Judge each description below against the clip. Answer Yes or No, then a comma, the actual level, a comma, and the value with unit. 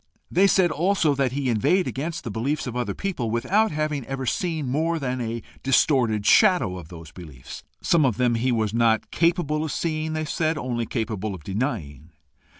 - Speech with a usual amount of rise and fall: No, wide, 5.9 semitones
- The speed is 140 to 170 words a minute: No, average, 185 wpm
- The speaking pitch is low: Yes, low, 130 Hz